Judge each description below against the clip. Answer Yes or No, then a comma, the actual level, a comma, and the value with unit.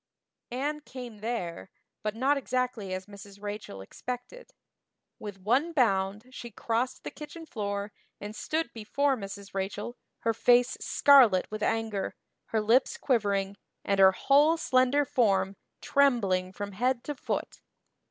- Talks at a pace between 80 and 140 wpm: Yes, slow, 135 wpm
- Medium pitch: No, high, 225 Hz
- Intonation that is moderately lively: Yes, average, 4.4 semitones